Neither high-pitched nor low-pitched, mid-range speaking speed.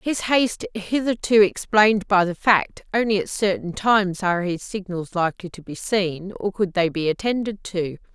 No: high, 195 Hz; average, 175 wpm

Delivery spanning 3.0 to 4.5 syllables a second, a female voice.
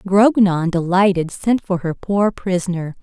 Yes: 4.1 syllables/s; female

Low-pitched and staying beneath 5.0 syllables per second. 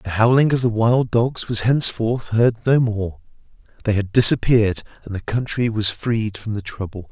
Yes: low, 110 Hz; 4.8 syllables/s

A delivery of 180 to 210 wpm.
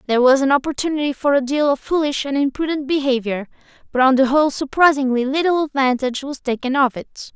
Yes: average, 190 wpm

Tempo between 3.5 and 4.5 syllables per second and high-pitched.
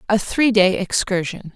Yes: 4.4 syllables/s; high, 200 Hz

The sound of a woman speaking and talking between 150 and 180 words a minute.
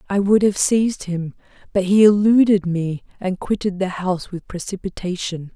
Yes: female; average, 160 wpm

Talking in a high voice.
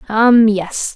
Yes: high, 215 Hz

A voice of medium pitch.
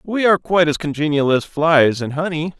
Yes: medium, 160 Hz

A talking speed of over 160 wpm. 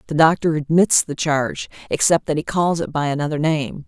Yes: average, 200 wpm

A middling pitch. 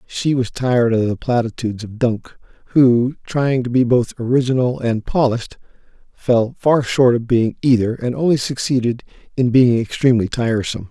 No: low, 120 Hz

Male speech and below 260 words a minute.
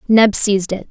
No: female; average, 200 wpm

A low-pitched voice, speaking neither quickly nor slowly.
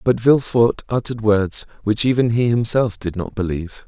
Yes: low, 110 Hz; average, 170 wpm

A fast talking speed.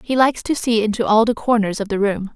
Yes: fast, 280 wpm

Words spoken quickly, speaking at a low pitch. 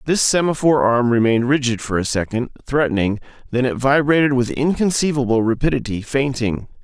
No: average, 140 wpm; low, 130 Hz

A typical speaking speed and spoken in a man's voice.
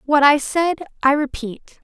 No: average, 165 wpm; female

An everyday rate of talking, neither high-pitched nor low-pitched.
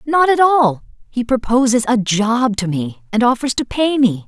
No: average, 195 wpm; high, 240 Hz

